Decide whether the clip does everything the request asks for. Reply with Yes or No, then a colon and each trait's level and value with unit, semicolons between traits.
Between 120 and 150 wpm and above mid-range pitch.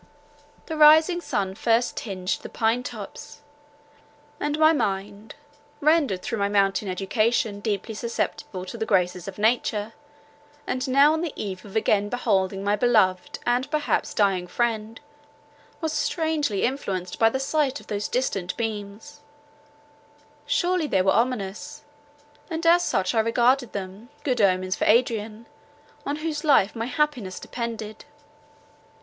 Yes: average, 140 wpm; high, 225 Hz